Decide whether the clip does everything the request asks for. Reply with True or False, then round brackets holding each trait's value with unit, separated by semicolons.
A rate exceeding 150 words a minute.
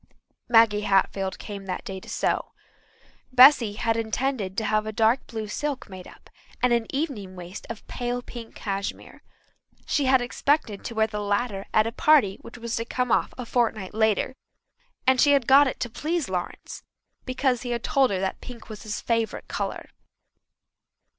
True (180 wpm)